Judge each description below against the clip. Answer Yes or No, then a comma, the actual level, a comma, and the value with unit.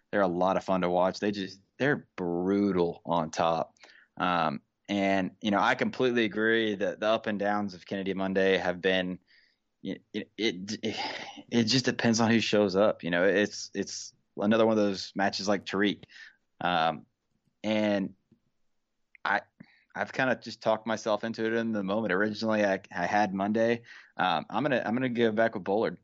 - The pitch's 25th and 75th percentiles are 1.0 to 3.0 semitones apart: Yes, narrow, 2.6 semitones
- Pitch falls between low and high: No, low, 100 Hz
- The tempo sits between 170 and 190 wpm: Yes, average, 175 wpm